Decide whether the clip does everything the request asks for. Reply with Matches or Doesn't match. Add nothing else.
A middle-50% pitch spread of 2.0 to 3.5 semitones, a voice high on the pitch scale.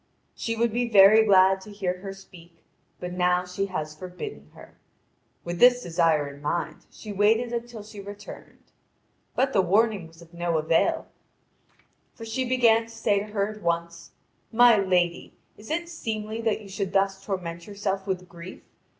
Doesn't match